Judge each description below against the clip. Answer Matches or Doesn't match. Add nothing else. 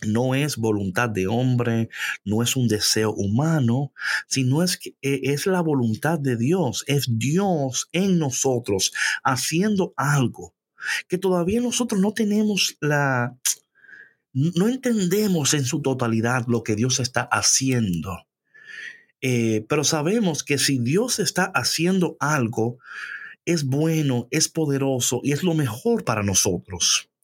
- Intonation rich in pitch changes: Matches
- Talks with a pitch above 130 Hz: Matches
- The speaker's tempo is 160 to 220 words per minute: Doesn't match